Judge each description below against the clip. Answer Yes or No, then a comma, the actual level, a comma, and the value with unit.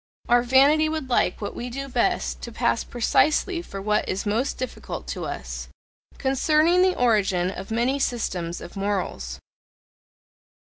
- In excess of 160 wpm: No, average, 145 wpm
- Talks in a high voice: Yes, high, 240 Hz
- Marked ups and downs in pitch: Yes, wide, 5.9 semitones